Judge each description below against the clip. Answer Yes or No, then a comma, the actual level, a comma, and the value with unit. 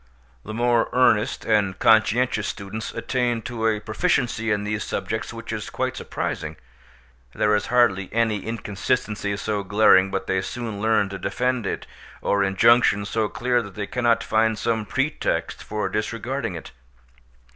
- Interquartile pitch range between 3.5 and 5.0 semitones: No, average, 2.7 semitones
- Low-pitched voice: Yes, low, 110 Hz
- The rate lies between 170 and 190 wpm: No, average, 150 wpm